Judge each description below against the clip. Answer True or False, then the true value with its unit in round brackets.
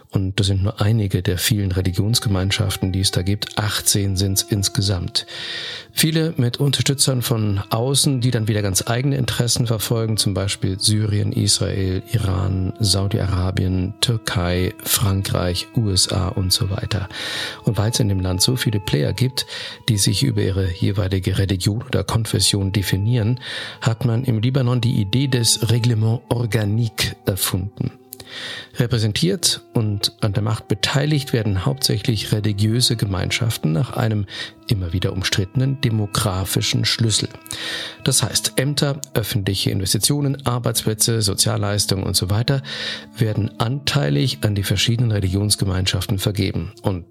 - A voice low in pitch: True (110 Hz)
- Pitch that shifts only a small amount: False (3.6 semitones)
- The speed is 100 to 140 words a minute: True (130 wpm)